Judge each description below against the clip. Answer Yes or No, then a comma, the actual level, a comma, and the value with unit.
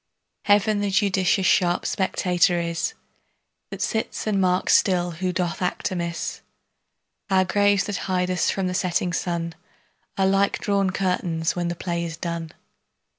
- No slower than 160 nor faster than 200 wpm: No, average, 150 wpm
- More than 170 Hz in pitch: Yes, medium, 185 Hz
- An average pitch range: No, narrow, 2.1 semitones